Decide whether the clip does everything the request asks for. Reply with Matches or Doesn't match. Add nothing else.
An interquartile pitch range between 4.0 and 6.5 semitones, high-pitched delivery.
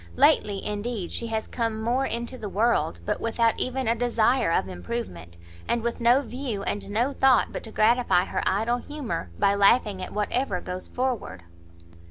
Doesn't match